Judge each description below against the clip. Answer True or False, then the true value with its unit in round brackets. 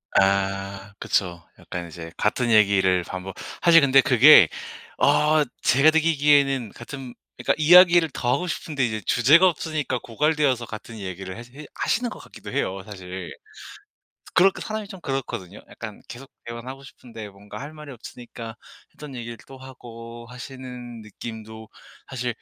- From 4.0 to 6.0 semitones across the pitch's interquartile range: True (5.5 semitones)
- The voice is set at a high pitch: False (120 Hz)